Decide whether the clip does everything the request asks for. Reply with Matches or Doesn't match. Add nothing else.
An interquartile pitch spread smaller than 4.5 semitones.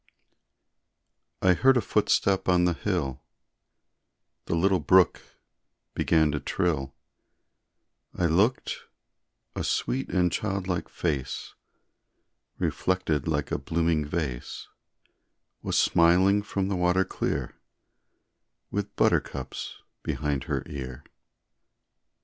Matches